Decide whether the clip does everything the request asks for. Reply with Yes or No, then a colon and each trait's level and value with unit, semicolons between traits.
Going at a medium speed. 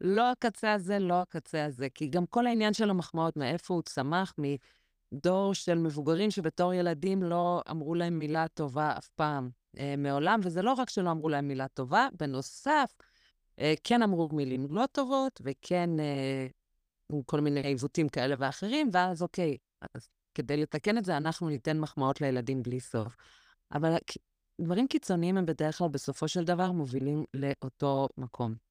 No: fast, 160 wpm